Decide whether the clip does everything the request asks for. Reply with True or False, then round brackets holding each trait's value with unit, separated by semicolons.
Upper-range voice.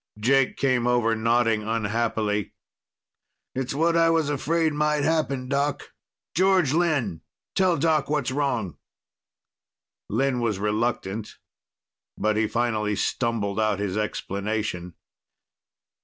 False (120 Hz)